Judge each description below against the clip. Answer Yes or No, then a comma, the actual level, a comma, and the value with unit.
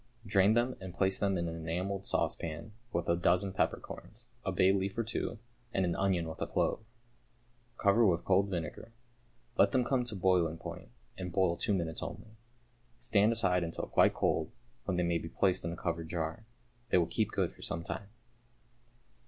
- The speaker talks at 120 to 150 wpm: No, average, 185 wpm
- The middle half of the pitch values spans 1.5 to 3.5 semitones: Yes, average, 2.8 semitones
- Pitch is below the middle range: Yes, very low, 95 Hz